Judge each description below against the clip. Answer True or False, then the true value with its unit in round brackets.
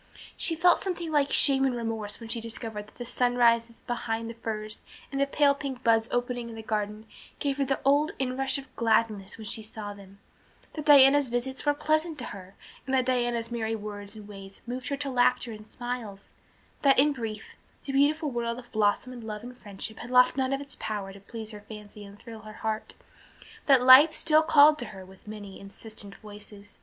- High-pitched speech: True (235 Hz)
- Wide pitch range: False (4.1 semitones)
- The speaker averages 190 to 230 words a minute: True (205 wpm)